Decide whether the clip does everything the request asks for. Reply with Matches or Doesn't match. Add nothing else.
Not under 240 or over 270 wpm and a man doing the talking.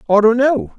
Doesn't match